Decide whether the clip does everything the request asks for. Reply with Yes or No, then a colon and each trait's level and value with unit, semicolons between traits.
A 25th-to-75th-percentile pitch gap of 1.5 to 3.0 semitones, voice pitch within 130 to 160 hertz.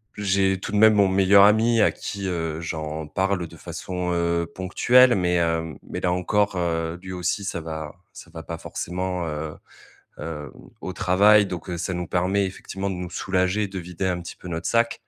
No: narrow, 2.6 semitones; very low, 90 Hz